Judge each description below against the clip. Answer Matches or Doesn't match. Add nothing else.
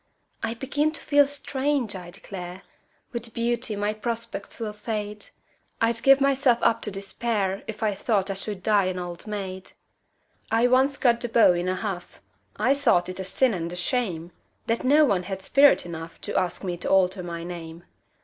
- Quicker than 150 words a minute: Matches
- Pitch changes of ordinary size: Matches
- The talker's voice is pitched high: Matches